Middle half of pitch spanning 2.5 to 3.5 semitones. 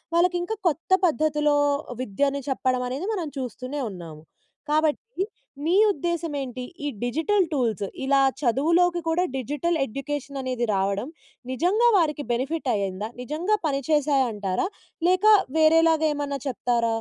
No: average, 4.6 semitones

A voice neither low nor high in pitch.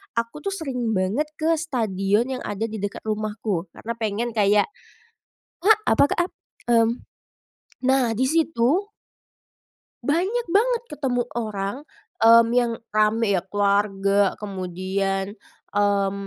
No: high, 225 Hz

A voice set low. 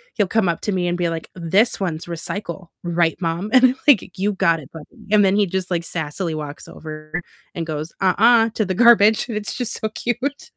No: medium, 185 Hz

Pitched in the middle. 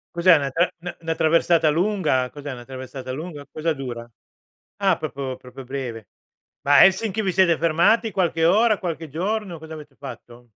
Yes: medium, 160 Hz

